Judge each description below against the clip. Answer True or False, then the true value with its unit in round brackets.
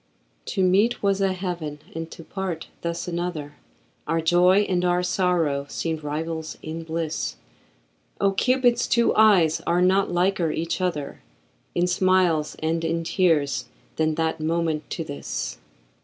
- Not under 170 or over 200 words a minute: False (140 wpm)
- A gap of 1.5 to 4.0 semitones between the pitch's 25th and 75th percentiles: True (2.5 semitones)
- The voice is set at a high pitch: False (170 Hz)